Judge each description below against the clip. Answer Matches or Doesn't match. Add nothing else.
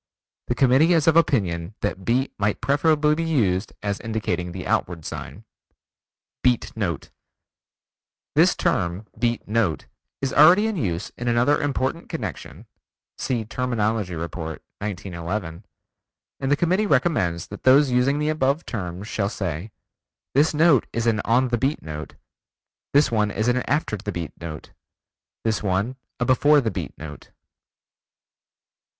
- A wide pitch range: Matches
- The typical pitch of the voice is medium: Doesn't match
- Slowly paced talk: Doesn't match